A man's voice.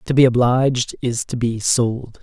Yes: male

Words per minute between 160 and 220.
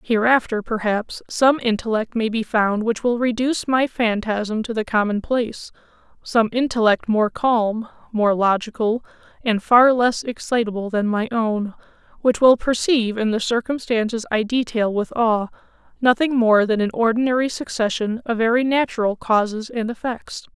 No: average, 145 wpm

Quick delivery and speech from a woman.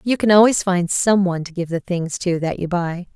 Yes: fast, 265 wpm; female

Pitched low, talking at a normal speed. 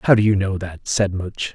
No: very low, 95 Hz; fast, 270 wpm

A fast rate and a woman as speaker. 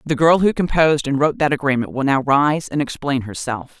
Yes: fast, 220 wpm; female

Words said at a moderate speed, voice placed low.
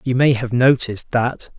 Yes: average, 190 wpm; low, 125 Hz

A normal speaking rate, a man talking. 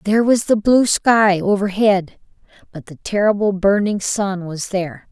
No: average, 150 wpm; female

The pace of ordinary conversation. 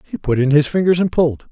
No: fast, 280 wpm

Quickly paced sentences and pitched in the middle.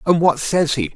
Yes: fast, 255 wpm; medium, 155 Hz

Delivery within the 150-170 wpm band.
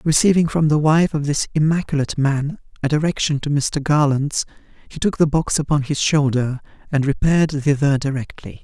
Yes: average, 165 wpm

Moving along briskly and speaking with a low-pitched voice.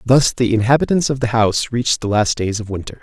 Yes: fast, 240 wpm; low, 115 Hz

